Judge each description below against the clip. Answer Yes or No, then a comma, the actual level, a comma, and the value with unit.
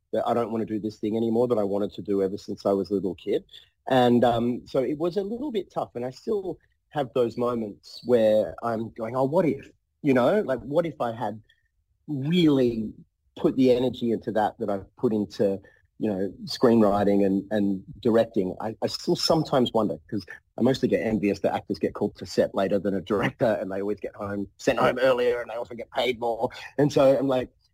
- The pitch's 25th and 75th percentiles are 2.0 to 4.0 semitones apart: Yes, average, 3.7 semitones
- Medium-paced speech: No, fast, 225 wpm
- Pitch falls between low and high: No, low, 115 Hz